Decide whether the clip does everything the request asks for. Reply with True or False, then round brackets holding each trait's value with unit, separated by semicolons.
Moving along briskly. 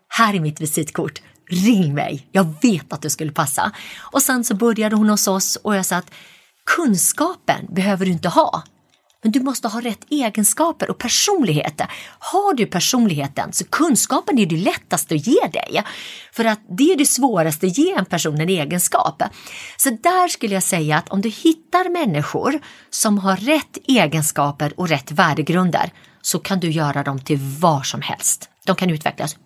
False (180 wpm)